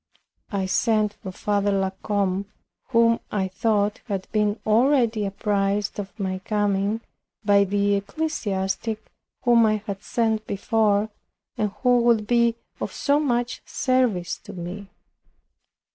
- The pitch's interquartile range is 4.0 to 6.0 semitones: No, narrow, 2.5 semitones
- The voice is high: Yes, high, 210 Hz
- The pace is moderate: No, slow, 130 wpm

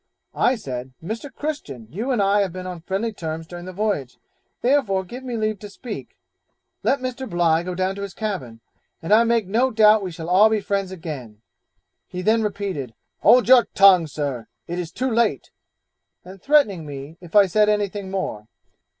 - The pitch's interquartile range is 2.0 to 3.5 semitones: No, average, 4.7 semitones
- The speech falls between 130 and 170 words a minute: No, average, 185 wpm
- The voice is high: Yes, high, 195 Hz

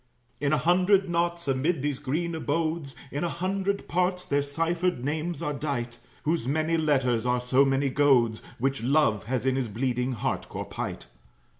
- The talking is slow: No, average, 170 wpm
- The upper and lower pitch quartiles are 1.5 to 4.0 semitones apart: No, average, 4.5 semitones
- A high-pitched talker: No, medium, 145 Hz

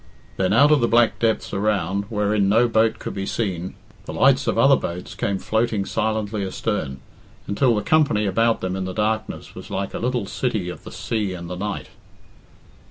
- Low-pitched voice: Yes, low, 105 Hz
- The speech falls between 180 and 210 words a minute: Yes, average, 190 wpm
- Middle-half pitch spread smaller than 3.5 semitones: Yes, average, 2.9 semitones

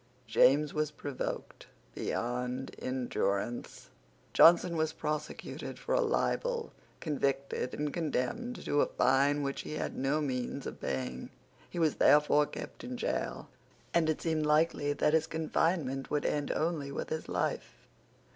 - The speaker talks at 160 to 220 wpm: No, average, 140 wpm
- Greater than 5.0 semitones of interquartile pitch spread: No, average, 3.0 semitones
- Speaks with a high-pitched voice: No, medium, 150 Hz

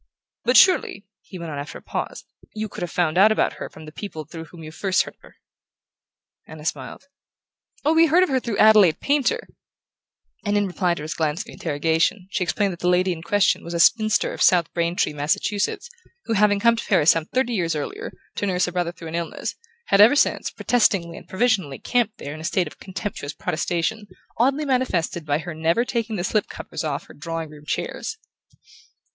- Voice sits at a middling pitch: Yes, medium, 180 Hz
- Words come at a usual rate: No, fast, 210 wpm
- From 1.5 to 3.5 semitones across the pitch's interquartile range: No, average, 5.1 semitones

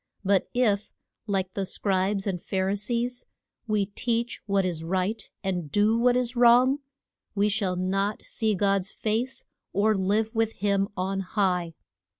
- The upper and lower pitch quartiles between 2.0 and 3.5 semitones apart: Yes, average, 2.7 semitones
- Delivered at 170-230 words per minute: No, average, 150 wpm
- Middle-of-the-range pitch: No, high, 200 Hz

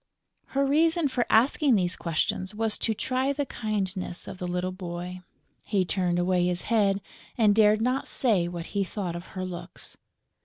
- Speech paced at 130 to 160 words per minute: No, average, 170 wpm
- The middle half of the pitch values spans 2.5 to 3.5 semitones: No, average, 4.5 semitones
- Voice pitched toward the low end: No, high, 195 Hz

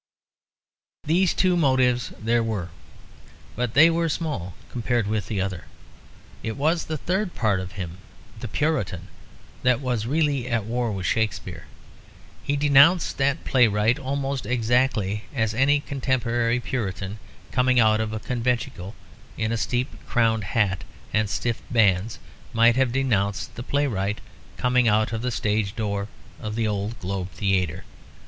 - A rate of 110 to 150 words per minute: Yes, average, 145 wpm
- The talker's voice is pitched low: Yes, low, 115 Hz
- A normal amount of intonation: Yes, average, 3.9 semitones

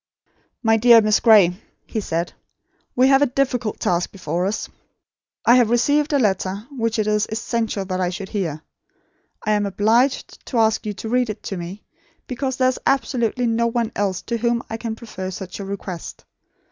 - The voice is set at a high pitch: Yes, high, 220 Hz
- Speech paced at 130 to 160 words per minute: No, average, 185 wpm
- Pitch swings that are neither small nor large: Yes, average, 3.6 semitones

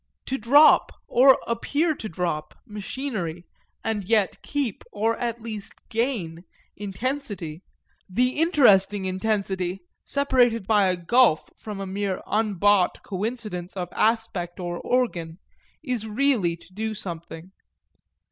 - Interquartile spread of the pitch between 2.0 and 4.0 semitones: No, average, 4.7 semitones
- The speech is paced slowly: Yes, slow, 120 wpm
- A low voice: No, high, 210 Hz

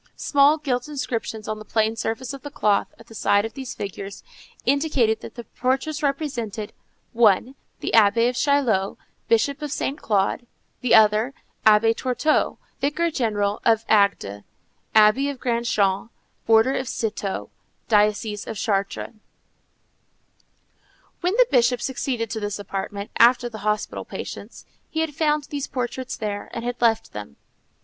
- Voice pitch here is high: Yes, high, 230 Hz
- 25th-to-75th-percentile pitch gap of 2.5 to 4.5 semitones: Yes, average, 4.1 semitones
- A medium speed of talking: Yes, average, 150 wpm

